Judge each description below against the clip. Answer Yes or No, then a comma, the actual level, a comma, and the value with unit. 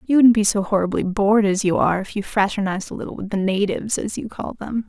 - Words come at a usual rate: No, fast, 260 wpm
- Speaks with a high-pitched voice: Yes, high, 205 Hz